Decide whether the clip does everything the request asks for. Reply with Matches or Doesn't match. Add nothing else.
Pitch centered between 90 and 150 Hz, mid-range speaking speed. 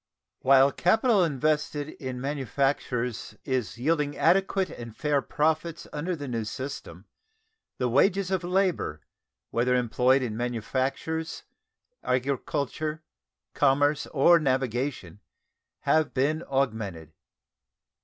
Doesn't match